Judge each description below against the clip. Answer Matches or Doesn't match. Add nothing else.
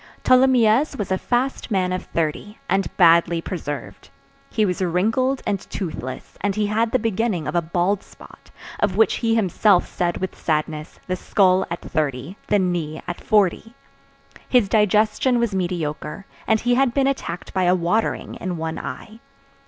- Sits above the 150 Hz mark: Matches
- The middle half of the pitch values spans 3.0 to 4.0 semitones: Doesn't match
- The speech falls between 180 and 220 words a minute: Doesn't match